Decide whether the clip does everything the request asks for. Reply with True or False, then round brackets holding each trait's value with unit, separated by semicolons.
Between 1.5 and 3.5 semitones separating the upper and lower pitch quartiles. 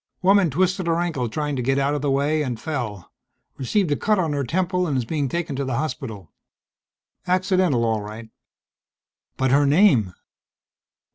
False (5.6 semitones)